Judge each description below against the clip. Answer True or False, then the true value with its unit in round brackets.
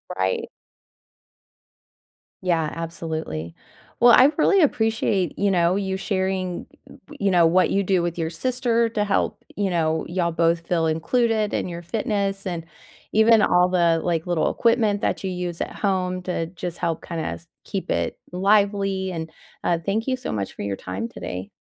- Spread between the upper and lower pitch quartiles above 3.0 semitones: True (3.4 semitones)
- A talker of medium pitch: True (180 Hz)